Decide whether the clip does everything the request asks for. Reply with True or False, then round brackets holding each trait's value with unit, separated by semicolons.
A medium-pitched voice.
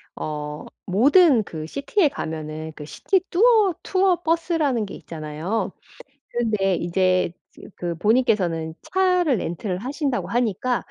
False (220 Hz)